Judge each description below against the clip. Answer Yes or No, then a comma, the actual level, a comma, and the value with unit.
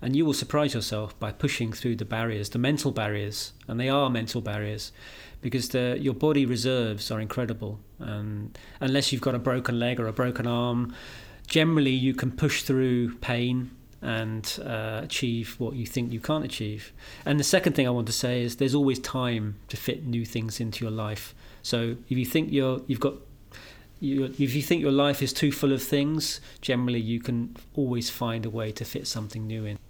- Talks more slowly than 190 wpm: No, average, 200 wpm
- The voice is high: No, low, 125 Hz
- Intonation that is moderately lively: Yes, average, 3.4 semitones